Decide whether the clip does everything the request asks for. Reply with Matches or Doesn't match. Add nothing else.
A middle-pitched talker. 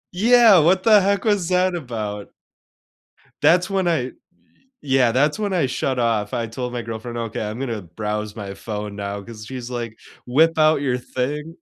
Doesn't match